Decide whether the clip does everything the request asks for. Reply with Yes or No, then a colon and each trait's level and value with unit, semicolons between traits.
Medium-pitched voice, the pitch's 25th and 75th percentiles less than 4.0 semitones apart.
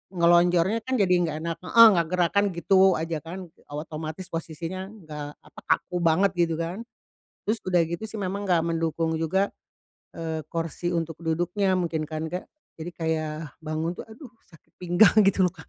Yes: medium, 170 Hz; narrow, 2.6 semitones